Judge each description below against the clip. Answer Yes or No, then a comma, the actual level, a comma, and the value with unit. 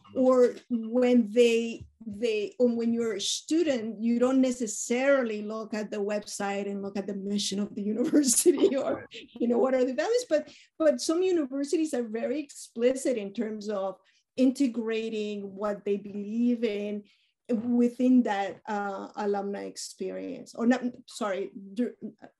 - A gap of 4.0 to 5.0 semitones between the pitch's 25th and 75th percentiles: No, average, 3.6 semitones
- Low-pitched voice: No, high, 230 Hz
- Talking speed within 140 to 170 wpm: Yes, average, 145 wpm